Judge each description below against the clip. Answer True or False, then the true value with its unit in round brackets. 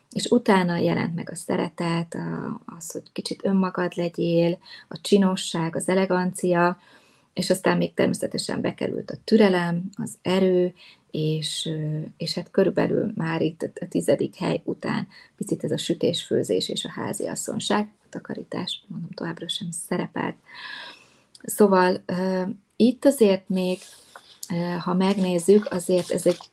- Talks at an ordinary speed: True (130 wpm)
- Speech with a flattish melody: True (1.8 semitones)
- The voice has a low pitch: False (180 Hz)